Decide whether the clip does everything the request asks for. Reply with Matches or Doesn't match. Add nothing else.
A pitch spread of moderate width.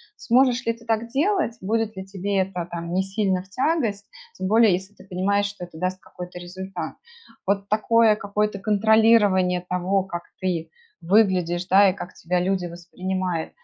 Matches